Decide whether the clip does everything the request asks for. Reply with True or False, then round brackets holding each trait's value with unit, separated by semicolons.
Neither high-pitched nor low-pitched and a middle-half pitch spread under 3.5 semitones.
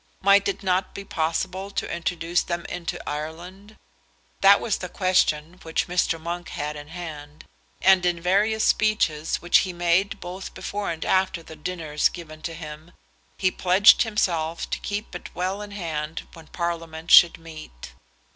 True (175 Hz; 2.9 semitones)